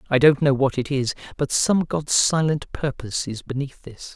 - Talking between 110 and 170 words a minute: No, average, 200 wpm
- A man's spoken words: Yes, male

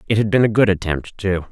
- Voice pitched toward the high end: No, low, 100 Hz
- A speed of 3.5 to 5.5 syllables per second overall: No, 6.0 syllables/s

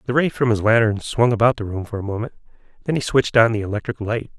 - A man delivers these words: Yes, male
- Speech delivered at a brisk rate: Yes, fast, 260 wpm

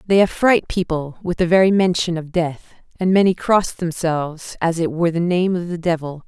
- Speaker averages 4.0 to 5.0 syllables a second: No, 5.2 syllables/s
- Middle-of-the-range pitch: Yes, medium, 175 Hz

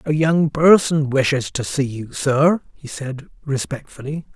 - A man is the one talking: Yes, male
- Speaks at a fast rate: No, average, 150 wpm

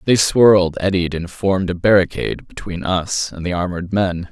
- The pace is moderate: Yes, average, 180 wpm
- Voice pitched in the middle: No, very low, 90 Hz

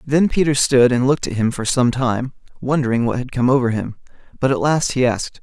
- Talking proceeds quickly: Yes, fast, 230 wpm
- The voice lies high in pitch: No, low, 130 Hz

